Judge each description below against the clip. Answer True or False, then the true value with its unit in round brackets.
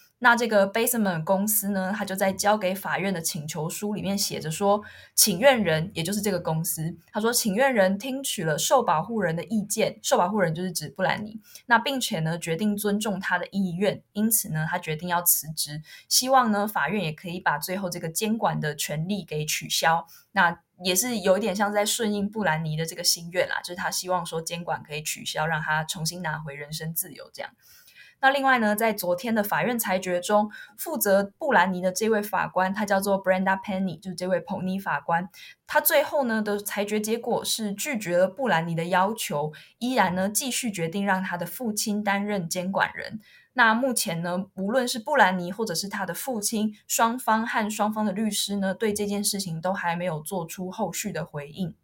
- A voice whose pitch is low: False (195 Hz)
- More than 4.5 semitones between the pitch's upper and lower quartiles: False (3.7 semitones)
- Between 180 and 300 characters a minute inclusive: False (315 characters per minute)